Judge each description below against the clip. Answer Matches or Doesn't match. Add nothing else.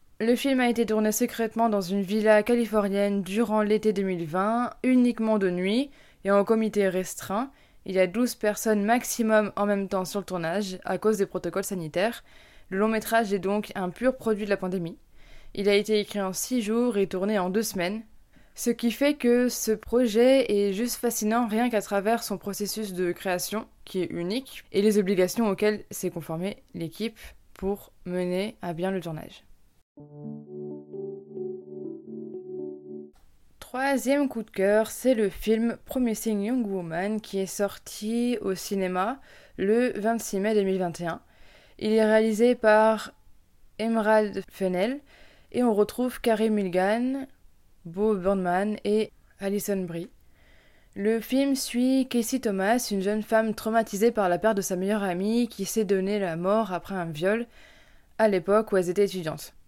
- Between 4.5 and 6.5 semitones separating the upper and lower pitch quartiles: Doesn't match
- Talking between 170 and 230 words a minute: Doesn't match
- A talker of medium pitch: Doesn't match